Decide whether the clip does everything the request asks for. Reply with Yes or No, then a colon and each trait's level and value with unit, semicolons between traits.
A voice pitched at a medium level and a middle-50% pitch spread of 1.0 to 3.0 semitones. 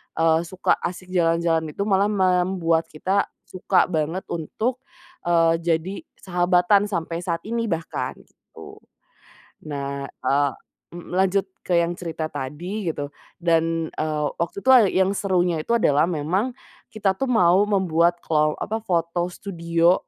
Yes: medium, 175 Hz; average, 2.7 semitones